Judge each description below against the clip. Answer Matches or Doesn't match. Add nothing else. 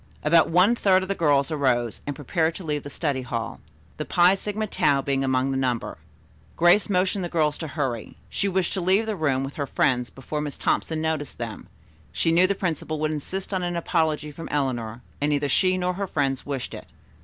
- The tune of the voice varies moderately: Matches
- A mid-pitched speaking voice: Matches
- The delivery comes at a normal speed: Doesn't match